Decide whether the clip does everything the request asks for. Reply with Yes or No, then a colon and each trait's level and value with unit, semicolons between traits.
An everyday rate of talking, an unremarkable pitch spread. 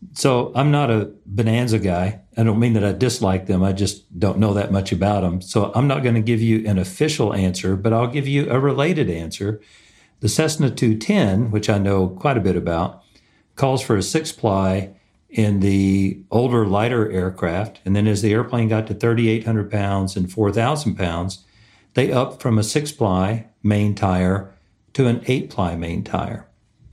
Yes: average, 185 wpm; average, 3.5 semitones